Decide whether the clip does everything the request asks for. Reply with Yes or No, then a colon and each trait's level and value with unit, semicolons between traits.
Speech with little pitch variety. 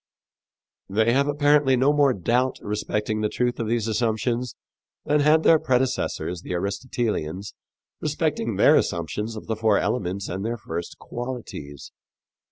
No: average, 4.4 semitones